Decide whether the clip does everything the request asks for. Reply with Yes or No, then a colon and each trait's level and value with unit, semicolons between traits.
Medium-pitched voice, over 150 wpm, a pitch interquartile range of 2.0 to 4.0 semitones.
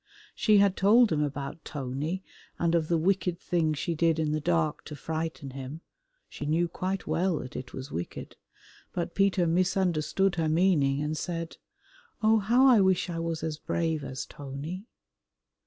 Yes: medium, 165 Hz; average, 170 wpm; average, 3.6 semitones